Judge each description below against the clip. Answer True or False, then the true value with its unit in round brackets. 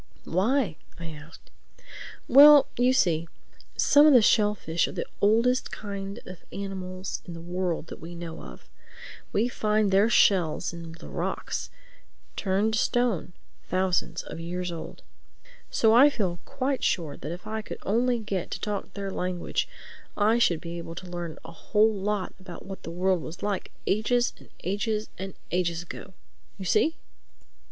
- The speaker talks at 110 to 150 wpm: False (160 wpm)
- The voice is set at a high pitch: True (195 Hz)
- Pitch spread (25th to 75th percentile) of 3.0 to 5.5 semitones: True (4.1 semitones)